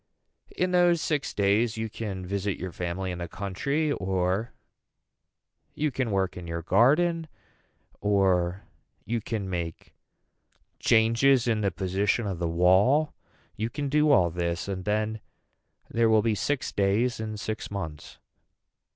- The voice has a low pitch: Yes, low, 105 Hz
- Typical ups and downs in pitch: Yes, average, 4.3 semitones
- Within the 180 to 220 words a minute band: No, average, 140 wpm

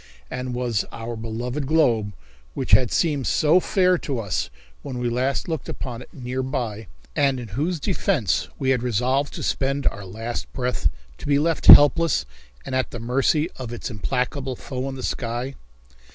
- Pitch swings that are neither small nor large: Yes, average, 3.1 semitones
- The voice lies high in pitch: No, low, 130 Hz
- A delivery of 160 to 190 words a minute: Yes, average, 175 wpm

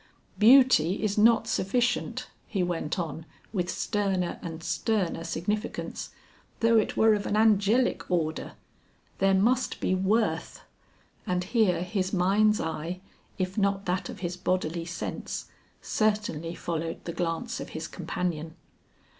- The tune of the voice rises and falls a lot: No, average, 3.7 semitones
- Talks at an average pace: No, slow, 130 wpm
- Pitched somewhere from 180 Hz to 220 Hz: Yes, medium, 185 Hz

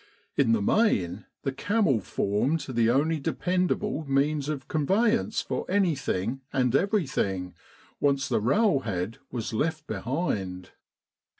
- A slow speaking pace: Yes, slow, 125 wpm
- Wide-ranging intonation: Yes, wide, 6.7 semitones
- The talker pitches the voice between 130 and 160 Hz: Yes, low, 135 Hz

